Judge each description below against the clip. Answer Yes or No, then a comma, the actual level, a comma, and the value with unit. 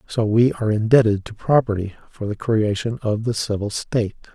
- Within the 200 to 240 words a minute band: No, average, 180 wpm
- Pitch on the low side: Yes, low, 110 Hz